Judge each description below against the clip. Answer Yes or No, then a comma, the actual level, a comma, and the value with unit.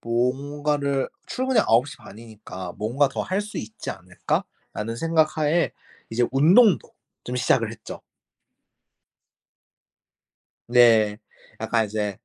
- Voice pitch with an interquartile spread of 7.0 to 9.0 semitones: No, average, 5.3 semitones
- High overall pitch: No, low, 125 Hz